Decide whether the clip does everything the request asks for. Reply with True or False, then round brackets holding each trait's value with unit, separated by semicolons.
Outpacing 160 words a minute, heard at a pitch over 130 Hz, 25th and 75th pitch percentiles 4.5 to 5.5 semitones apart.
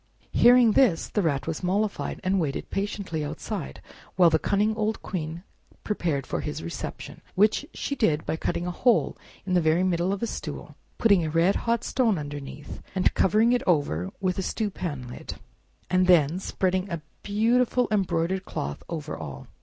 True (170 wpm; 185 Hz; 5.0 semitones)